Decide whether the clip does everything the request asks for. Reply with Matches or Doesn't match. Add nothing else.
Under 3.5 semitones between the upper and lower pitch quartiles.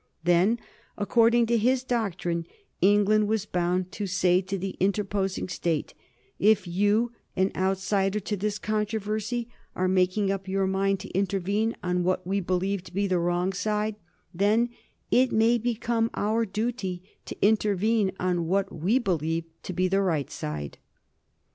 Matches